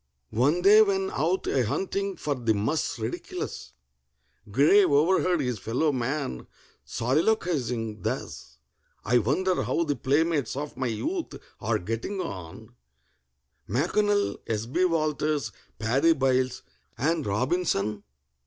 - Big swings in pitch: Yes, wide, 7.2 semitones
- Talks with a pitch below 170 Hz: Yes, medium, 140 Hz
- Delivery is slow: Yes, slow, 115 wpm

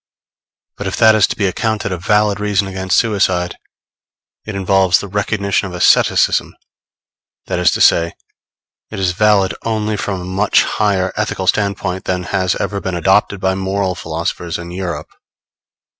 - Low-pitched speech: Yes, very low, 95 Hz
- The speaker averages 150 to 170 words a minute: Yes, average, 160 wpm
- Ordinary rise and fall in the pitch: No, narrow, 2.1 semitones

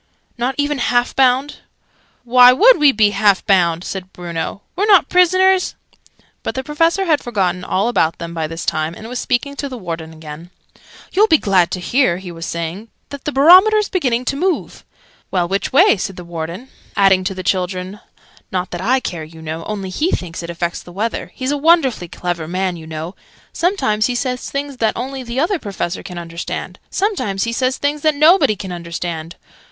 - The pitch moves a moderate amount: No, wide, 8.2 semitones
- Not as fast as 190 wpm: No, average, 195 wpm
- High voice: Yes, high, 210 Hz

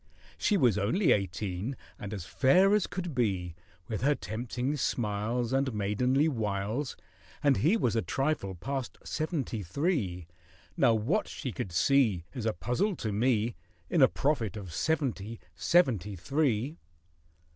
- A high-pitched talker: No, low, 120 Hz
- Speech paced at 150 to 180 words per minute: No, average, 140 wpm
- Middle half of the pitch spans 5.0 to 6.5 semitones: Yes, wide, 5.6 semitones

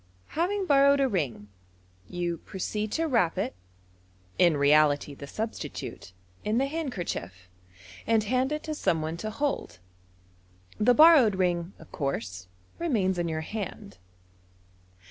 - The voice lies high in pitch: Yes, high, 200 Hz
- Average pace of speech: No, slow, 130 wpm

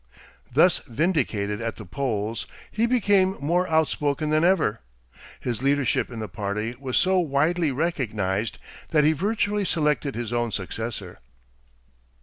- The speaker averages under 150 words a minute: Yes, slow, 135 wpm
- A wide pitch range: Yes, wide, 7.1 semitones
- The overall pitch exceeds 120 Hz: Yes, medium, 140 Hz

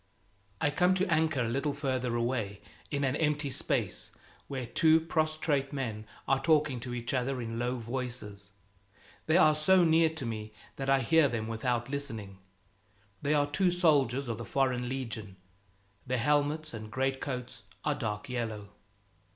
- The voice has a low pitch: Yes, low, 130 Hz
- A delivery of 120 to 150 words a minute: No, average, 160 wpm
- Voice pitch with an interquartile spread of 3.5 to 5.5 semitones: Yes, average, 4.1 semitones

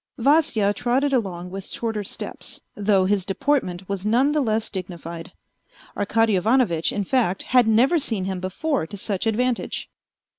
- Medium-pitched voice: No, high, 210 Hz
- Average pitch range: Yes, average, 4.9 semitones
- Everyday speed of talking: Yes, average, 150 wpm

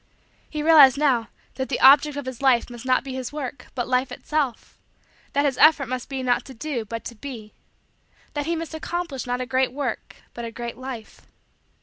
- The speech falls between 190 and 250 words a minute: Yes, fast, 205 wpm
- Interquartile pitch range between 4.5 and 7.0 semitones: No, average, 2.9 semitones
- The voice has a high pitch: Yes, very high, 260 Hz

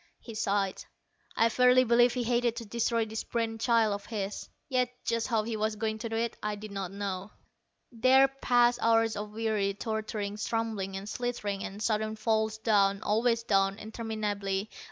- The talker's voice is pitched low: No, high, 220 Hz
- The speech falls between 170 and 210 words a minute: Yes, average, 175 wpm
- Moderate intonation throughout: No, narrow, 2.1 semitones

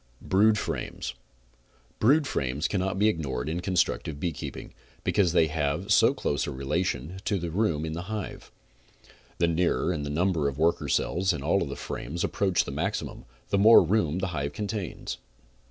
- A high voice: No, very low, 85 Hz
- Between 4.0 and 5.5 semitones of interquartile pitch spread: Yes, average, 4.6 semitones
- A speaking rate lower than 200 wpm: Yes, average, 160 wpm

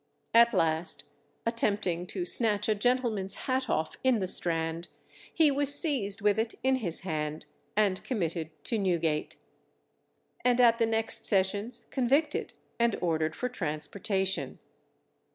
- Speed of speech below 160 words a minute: Yes, slow, 135 wpm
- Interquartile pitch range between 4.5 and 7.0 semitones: Yes, wide, 5.5 semitones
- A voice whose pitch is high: Yes, high, 205 Hz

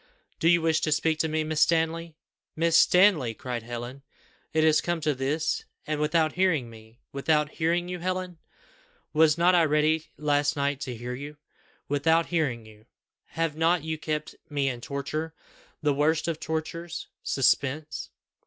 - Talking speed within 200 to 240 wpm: No, average, 165 wpm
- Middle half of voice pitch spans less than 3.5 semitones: Yes, average, 2.7 semitones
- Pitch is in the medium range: Yes, medium, 155 Hz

